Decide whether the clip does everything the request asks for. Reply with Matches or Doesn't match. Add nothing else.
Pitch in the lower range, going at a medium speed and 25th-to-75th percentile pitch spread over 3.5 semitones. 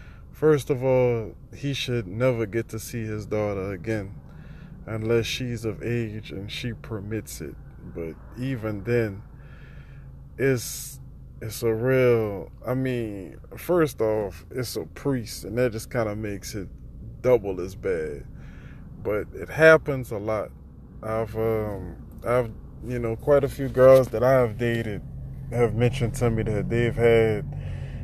Doesn't match